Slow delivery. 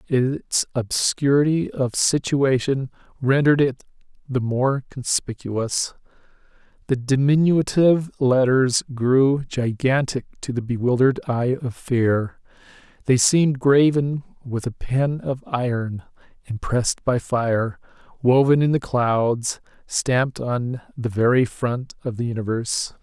Yes: slow, 110 wpm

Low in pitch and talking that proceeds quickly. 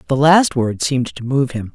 Yes: low, 130 Hz; fast, 240 wpm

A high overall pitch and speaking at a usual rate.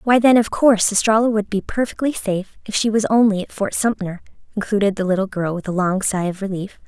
No: high, 205 Hz; fast, 225 wpm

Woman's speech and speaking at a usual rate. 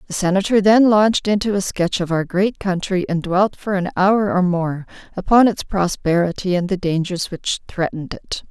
Yes: female; average, 190 wpm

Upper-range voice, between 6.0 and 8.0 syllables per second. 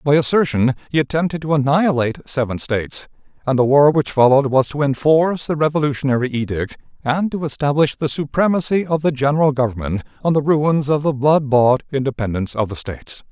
No: medium, 140 Hz; 6.1 syllables/s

